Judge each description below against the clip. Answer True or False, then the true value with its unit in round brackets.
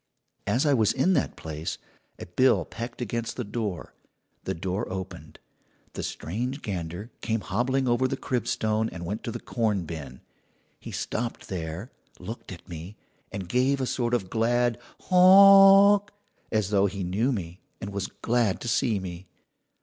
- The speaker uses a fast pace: False (165 wpm)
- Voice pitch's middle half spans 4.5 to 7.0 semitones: True (4.8 semitones)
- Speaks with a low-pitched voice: True (110 Hz)